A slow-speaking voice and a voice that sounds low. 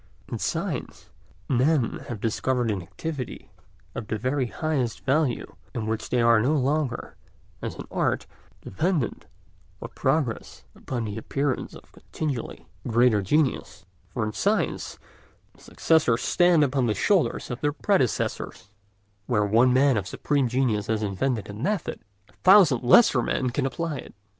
No: average, 150 wpm; low, 125 Hz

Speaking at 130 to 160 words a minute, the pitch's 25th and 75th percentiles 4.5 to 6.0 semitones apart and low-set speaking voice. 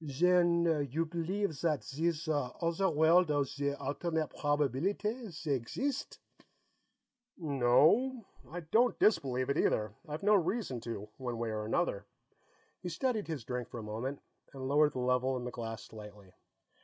No: average, 150 wpm; wide, 5.4 semitones; medium, 150 Hz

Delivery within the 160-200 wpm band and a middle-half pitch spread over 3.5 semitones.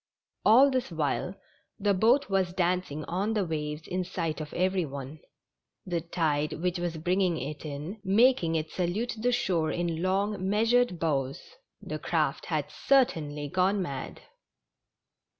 No: average, 150 wpm; average, 4.2 semitones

